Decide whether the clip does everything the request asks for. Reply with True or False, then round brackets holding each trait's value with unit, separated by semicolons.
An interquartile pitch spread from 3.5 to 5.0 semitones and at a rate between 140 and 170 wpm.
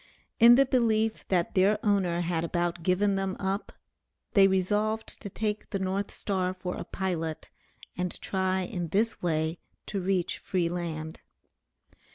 False (2.7 semitones; 150 wpm)